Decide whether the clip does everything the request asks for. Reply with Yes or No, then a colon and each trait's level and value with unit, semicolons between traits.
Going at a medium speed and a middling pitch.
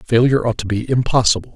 No: average, 195 wpm; low, 120 Hz